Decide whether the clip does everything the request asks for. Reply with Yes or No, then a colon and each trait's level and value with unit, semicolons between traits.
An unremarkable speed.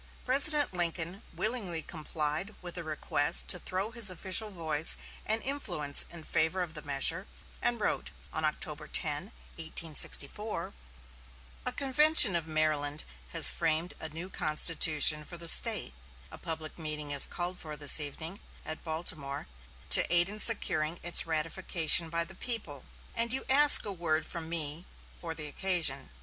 Yes: average, 150 wpm